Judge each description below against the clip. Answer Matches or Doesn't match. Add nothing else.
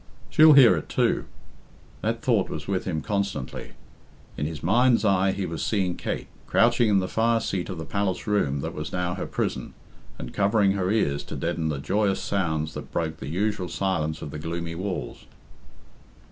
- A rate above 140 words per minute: Matches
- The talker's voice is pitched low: Matches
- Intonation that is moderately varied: Matches